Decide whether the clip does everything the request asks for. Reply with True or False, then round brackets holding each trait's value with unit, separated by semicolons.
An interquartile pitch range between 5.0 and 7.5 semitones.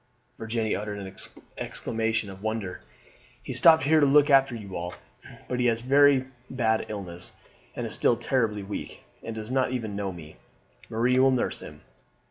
False (4.2 semitones)